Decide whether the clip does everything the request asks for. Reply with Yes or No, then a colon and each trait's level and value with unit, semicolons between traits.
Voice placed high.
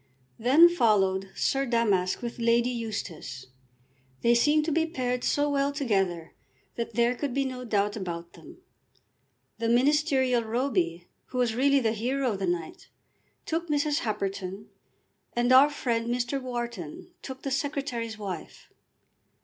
Yes: high, 240 Hz